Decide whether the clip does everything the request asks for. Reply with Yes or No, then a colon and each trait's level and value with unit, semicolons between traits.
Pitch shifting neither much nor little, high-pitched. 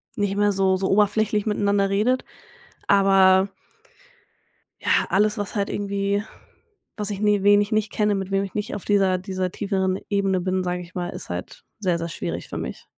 No: narrow, 1.5 semitones; high, 200 Hz